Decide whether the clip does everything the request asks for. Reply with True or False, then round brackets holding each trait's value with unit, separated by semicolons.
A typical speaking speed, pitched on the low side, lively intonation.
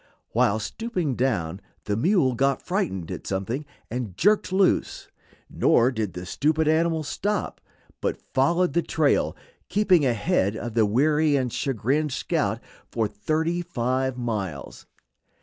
False (130 wpm; 130 Hz; 6.6 semitones)